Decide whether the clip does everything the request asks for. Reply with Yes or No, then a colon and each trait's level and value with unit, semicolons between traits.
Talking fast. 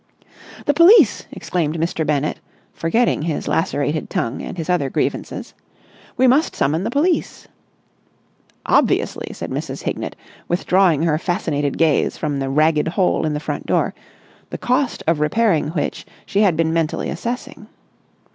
No: average, 145 wpm